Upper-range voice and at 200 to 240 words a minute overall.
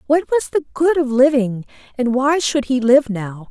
Yes: very high, 255 Hz; fast, 205 wpm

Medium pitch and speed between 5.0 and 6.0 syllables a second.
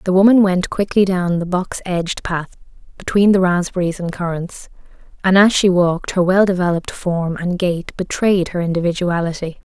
Yes: medium, 180 Hz; 5.2 syllables/s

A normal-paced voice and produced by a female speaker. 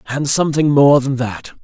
No: average, 185 wpm; male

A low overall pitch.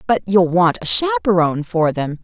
No: medium, 185 Hz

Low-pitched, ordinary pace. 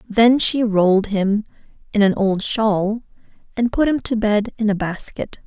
No: high, 215 Hz; average, 175 wpm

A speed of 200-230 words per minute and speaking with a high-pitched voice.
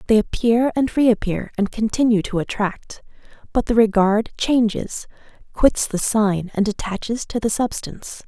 No: average, 145 wpm; high, 220 Hz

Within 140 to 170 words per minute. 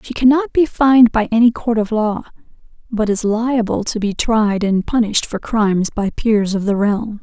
No: average, 200 wpm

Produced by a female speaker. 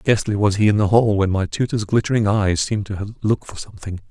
No: male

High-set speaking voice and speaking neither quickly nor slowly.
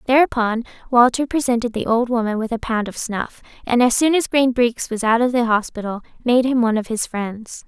No: high, 235 Hz; fast, 220 wpm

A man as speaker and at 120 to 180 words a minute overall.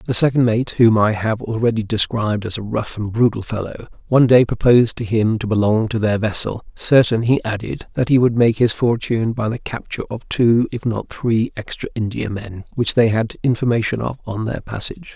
No: male; average, 200 wpm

